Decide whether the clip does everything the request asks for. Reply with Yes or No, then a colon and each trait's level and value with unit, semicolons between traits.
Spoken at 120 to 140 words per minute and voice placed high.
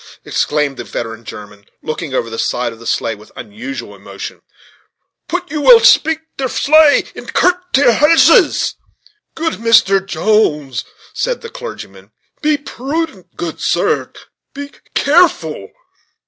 Yes: slow, 135 wpm; high, 230 Hz